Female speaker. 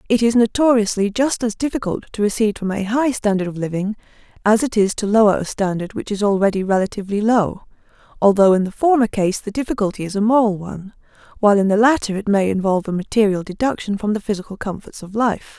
Yes: female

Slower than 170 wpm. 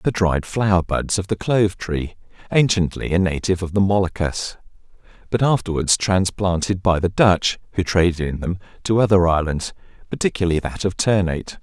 Yes: average, 160 wpm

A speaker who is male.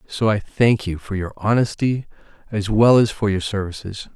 Yes: male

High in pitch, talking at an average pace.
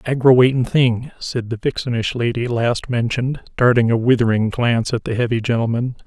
No: low, 120 Hz; average, 160 wpm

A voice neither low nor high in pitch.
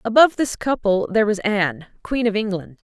No: high, 215 Hz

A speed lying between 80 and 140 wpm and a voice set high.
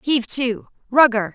Yes: slow, 135 wpm; high, 240 Hz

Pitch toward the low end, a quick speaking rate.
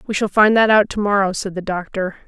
No: high, 200 Hz; fast, 265 wpm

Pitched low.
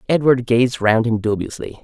Yes: low, 120 Hz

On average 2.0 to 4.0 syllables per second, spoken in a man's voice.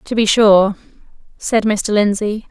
No: 3.9 syllables/s; female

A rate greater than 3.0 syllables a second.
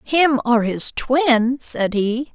No: 2.8 syllables/s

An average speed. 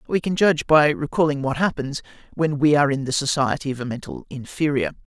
Yes: average, 195 wpm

